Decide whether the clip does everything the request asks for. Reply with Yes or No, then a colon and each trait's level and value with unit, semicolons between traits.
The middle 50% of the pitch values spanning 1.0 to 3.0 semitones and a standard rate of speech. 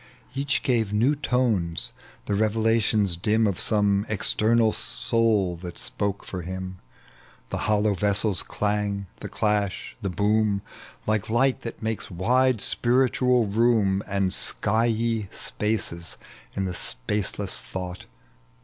No: average, 2.7 semitones; slow, 120 wpm